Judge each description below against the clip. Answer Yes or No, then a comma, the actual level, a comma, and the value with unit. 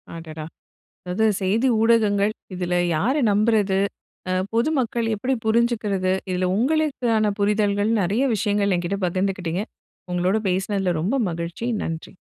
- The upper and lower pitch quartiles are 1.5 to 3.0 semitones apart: No, average, 3.6 semitones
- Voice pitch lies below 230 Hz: Yes, high, 205 Hz